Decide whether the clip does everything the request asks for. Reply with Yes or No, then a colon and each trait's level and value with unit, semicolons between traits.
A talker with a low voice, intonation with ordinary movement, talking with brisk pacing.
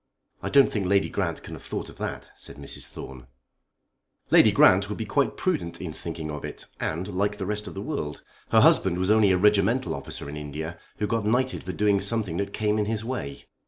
Yes: low, 100 Hz; average, 4.0 semitones; fast, 220 wpm